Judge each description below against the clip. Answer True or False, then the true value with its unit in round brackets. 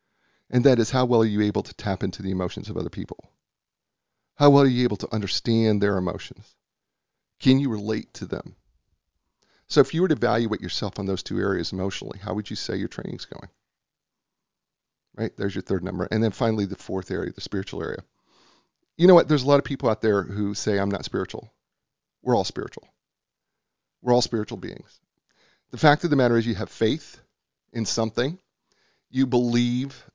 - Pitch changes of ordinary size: True (4.0 semitones)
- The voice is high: False (110 Hz)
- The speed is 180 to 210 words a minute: True (195 wpm)